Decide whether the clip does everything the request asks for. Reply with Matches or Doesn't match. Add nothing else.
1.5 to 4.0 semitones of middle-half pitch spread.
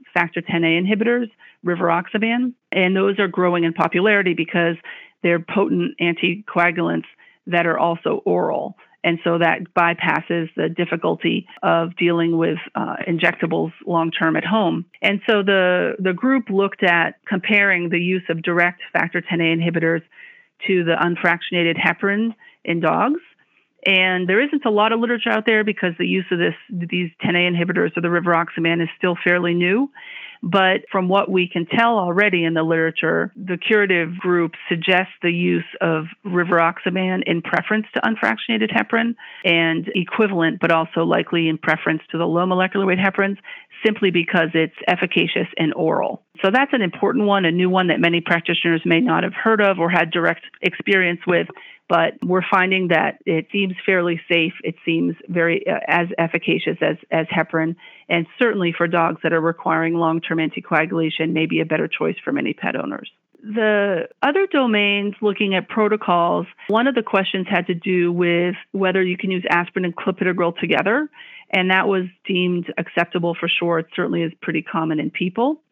Matches